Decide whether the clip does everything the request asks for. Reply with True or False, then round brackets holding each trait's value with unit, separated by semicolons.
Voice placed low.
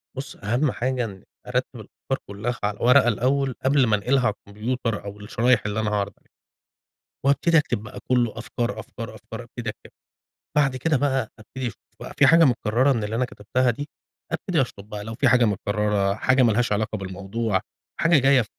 True (120 Hz)